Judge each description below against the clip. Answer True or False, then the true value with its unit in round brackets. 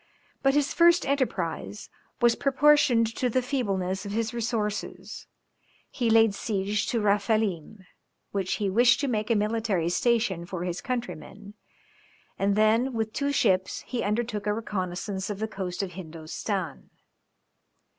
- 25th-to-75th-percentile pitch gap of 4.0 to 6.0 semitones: False (3.6 semitones)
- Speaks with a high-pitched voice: True (215 Hz)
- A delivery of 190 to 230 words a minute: False (140 wpm)